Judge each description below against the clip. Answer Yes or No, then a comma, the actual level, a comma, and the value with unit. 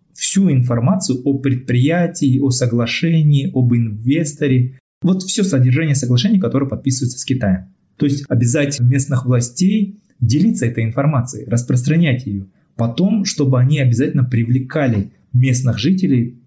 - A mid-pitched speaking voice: No, low, 130 Hz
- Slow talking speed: No, average, 120 wpm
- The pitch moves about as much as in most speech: Yes, average, 3.7 semitones